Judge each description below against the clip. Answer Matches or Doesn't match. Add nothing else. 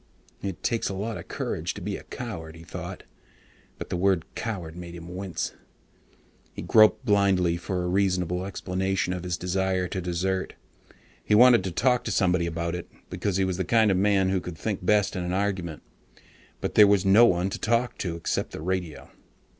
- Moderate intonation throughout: Doesn't match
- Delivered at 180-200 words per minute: Matches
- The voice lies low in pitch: Matches